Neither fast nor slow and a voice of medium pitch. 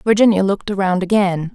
No: average, 155 wpm; high, 195 Hz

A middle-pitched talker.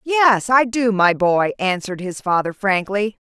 No: high, 205 Hz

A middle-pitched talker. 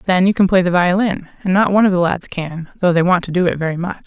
Yes: medium, 180 Hz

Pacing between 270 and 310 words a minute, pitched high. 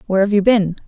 Yes: fast, 275 wpm; high, 200 Hz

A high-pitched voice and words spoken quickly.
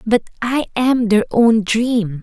No: high, 225 Hz; average, 160 wpm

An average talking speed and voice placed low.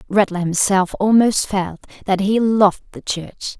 No: average, 150 wpm; high, 200 Hz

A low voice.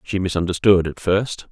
Yes: very low, 95 Hz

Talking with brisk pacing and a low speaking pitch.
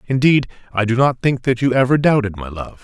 Yes: fast, 235 wpm; low, 125 Hz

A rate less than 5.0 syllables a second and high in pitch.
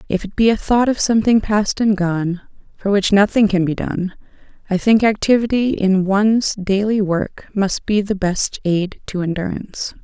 Yes: 4.7 syllables/s; high, 200 Hz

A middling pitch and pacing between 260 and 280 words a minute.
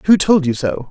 Yes: medium, 155 Hz; fast, 265 wpm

